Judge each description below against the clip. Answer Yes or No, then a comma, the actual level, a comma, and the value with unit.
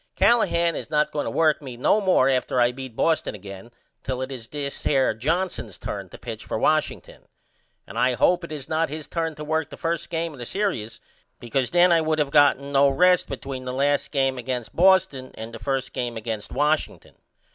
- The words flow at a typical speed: No, fast, 210 wpm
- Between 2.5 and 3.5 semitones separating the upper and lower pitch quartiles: No, average, 4.2 semitones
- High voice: No, medium, 140 Hz